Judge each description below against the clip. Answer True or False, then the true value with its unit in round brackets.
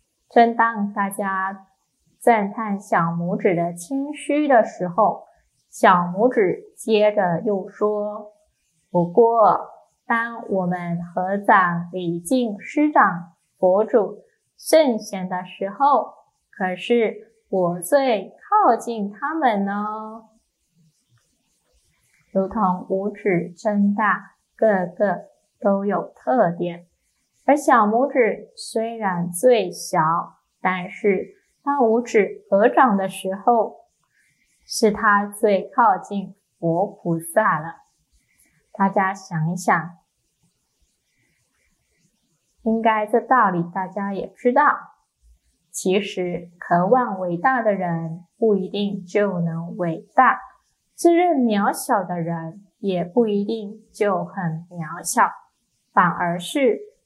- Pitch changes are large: False (4.3 semitones)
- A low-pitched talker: False (200 Hz)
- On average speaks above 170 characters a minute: False (145 characters per minute)